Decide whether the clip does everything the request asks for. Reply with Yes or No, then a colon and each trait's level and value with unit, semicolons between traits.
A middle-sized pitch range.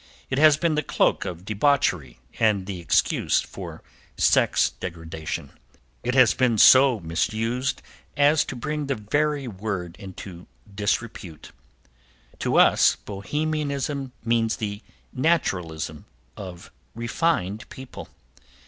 No: wide, 6.9 semitones